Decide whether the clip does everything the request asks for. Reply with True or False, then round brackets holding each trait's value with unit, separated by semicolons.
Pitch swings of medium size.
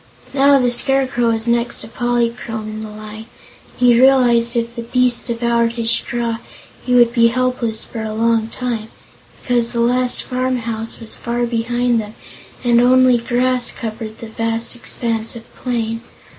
False (1.4 semitones)